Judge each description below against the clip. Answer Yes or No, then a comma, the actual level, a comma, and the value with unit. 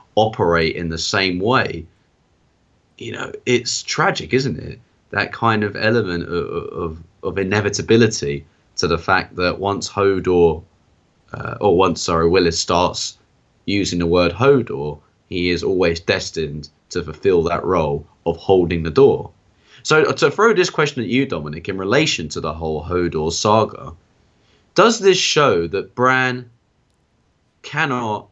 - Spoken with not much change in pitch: No, wide, 5.6 semitones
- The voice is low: Yes, very low, 95 Hz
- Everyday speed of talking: Yes, average, 145 wpm